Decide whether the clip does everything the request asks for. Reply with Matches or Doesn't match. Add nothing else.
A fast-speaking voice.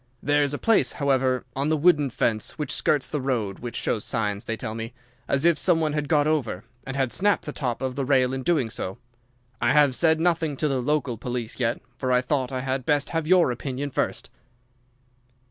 Matches